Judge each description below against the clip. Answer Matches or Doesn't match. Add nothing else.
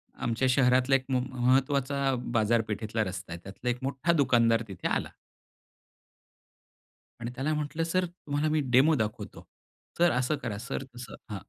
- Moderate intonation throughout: Matches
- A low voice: Matches